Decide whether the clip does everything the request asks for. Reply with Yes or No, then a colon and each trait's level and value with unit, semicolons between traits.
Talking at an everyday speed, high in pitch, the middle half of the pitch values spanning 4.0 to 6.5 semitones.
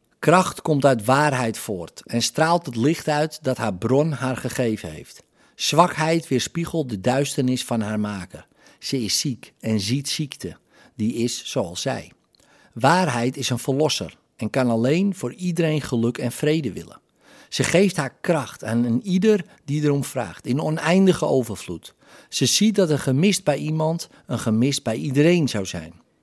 No: average, 165 wpm; low, 135 Hz; average, 5.0 semitones